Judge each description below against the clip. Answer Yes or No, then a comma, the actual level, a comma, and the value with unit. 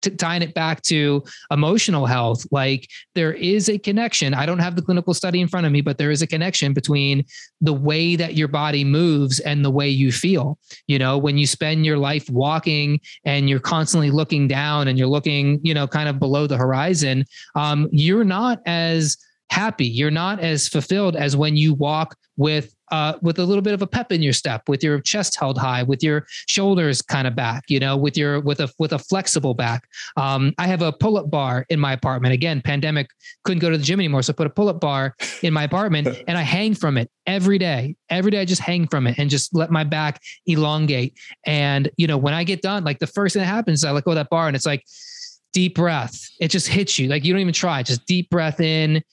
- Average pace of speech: No, fast, 235 wpm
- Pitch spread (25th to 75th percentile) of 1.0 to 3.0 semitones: No, average, 3.6 semitones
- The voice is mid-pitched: Yes, medium, 155 Hz